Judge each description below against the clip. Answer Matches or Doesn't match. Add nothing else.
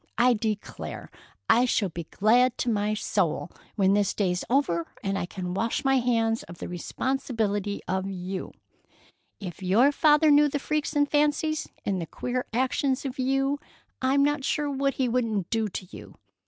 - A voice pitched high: Matches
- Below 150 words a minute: Doesn't match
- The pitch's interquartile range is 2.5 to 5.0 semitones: Doesn't match